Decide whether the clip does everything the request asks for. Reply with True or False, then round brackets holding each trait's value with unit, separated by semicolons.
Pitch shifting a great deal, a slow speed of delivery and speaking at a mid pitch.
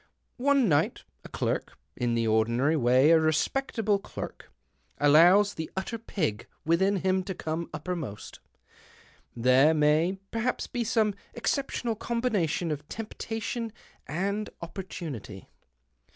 True (6.3 semitones; 125 wpm; 175 Hz)